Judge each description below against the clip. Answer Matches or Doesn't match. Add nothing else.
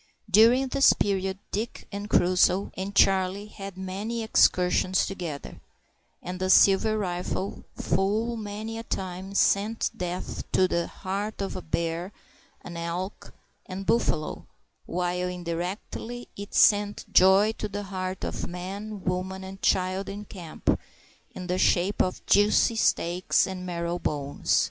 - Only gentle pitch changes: Matches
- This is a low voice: Doesn't match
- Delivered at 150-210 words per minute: Doesn't match